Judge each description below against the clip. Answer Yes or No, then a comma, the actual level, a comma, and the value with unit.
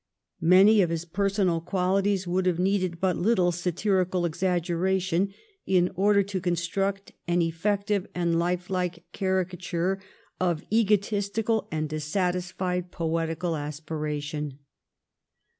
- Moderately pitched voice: Yes, medium, 180 Hz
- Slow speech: Yes, slow, 110 wpm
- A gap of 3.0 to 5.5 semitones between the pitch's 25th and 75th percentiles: No, narrow, 2.4 semitones